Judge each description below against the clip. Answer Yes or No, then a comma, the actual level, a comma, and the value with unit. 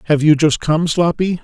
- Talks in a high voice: No, medium, 160 Hz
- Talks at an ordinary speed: No, fast, 210 wpm